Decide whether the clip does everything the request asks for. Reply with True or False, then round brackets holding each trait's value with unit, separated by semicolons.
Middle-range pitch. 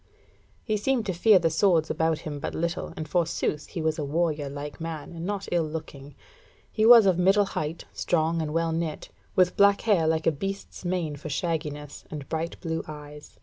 True (165 Hz)